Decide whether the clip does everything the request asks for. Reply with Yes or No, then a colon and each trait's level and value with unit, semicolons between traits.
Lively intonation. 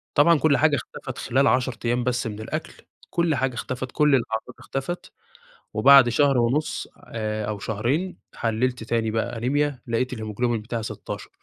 No: average, 3.6 semitones